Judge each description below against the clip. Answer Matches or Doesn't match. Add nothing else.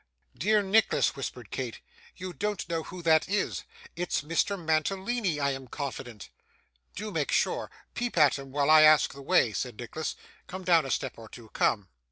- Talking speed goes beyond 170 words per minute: Matches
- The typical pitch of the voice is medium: Matches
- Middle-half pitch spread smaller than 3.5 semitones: Doesn't match